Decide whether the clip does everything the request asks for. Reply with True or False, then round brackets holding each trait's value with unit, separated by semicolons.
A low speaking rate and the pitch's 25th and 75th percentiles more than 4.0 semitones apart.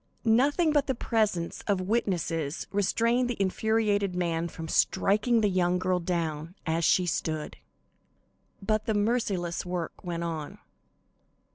True (130 wpm; 4.5 semitones)